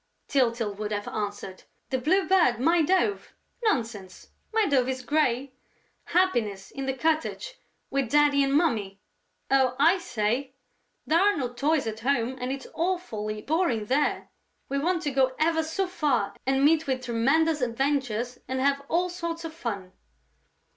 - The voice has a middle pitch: No, very high, 275 Hz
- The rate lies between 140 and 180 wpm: Yes, average, 155 wpm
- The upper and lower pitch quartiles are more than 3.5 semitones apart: Yes, average, 5.3 semitones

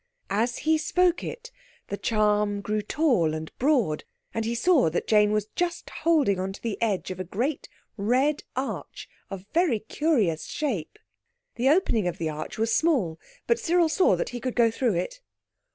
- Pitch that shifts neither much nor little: No, wide, 7.5 semitones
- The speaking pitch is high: Yes, high, 230 Hz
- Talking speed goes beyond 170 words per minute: Yes, average, 180 wpm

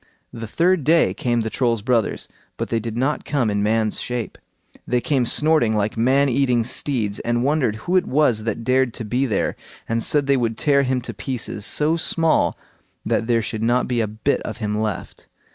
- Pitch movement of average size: Yes, average, 3.6 semitones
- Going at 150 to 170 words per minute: No, average, 200 wpm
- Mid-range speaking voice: No, low, 120 Hz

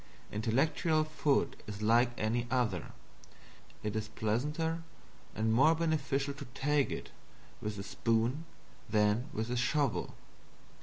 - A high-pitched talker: No, low, 125 Hz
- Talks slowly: Yes, slow, 120 wpm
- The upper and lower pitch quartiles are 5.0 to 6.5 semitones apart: Yes, average, 5.3 semitones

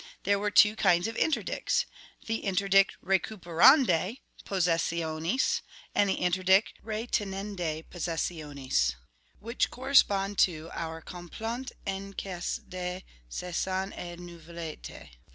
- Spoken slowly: Yes, slow, 100 wpm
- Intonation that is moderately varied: Yes, average, 3.2 semitones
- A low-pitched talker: No, medium, 185 Hz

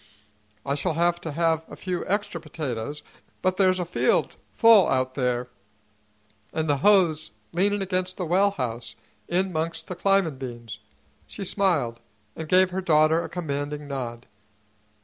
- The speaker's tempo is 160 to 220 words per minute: No, average, 150 wpm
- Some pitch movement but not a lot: Yes, average, 4.8 semitones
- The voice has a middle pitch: Yes, medium, 165 Hz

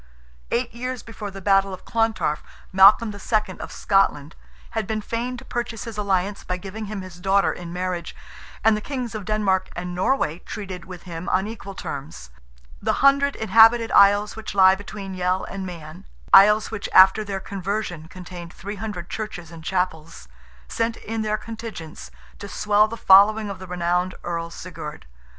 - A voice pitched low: No, high, 195 Hz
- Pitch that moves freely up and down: No, average, 3.4 semitones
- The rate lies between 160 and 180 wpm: Yes, average, 165 wpm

